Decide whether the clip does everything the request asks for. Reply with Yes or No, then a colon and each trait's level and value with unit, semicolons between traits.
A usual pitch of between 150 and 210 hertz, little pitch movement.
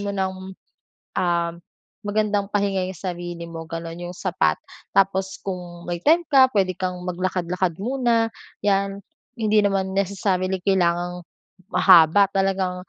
Yes: high, 190 Hz; narrow, 2.3 semitones